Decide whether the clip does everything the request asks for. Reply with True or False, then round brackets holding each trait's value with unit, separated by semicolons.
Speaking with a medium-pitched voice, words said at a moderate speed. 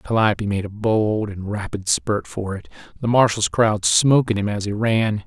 False (105 Hz; 195 wpm)